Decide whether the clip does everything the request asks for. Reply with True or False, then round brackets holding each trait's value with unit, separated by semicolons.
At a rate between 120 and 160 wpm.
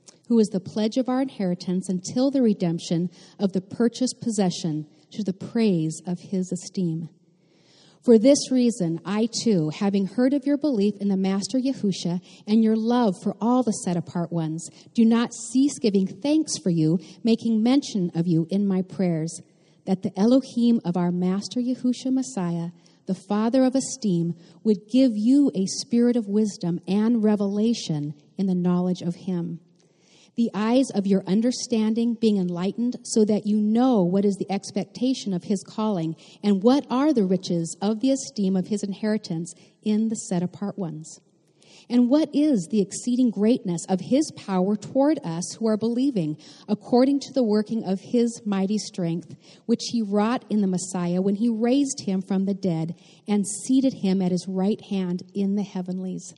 False (170 wpm)